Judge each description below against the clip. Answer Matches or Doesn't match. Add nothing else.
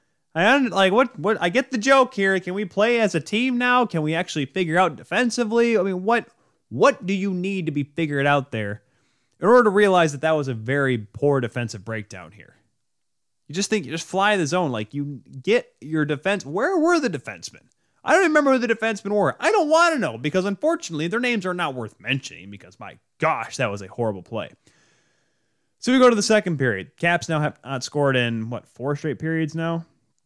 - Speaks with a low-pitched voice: Doesn't match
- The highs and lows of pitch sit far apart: Matches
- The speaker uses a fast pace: Matches